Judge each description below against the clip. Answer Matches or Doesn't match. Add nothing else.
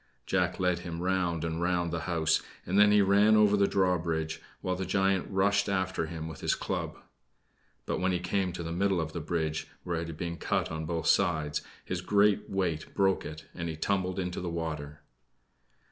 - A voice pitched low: Matches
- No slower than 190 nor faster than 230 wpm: Matches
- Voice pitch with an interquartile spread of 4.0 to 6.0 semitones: Doesn't match